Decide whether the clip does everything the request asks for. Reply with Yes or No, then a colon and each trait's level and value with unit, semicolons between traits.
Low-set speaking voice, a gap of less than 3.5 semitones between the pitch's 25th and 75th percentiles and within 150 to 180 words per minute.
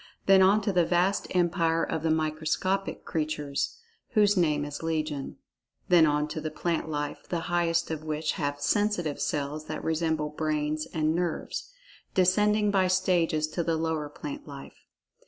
No: medium, 160 Hz; average, 2.8 semitones; average, 155 wpm